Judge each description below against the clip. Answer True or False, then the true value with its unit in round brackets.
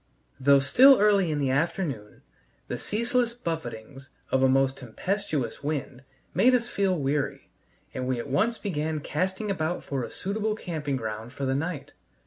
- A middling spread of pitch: False (7.0 semitones)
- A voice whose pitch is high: False (150 Hz)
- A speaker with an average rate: True (160 wpm)